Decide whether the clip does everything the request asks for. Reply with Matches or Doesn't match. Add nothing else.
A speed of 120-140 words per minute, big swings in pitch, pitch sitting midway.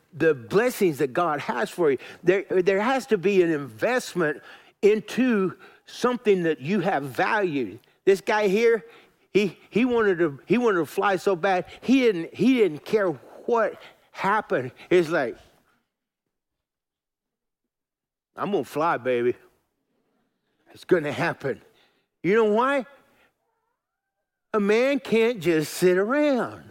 Doesn't match